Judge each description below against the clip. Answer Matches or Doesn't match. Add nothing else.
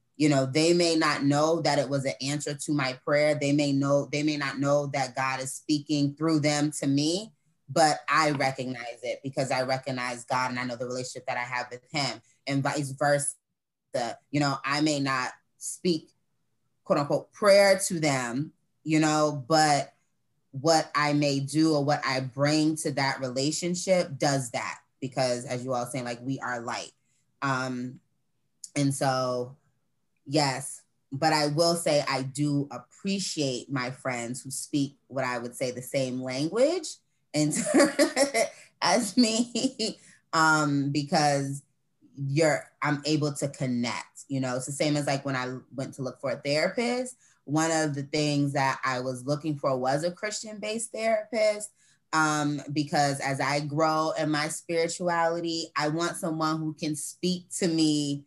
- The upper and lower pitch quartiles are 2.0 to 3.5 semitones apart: Matches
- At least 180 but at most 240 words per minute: Doesn't match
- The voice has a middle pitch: Matches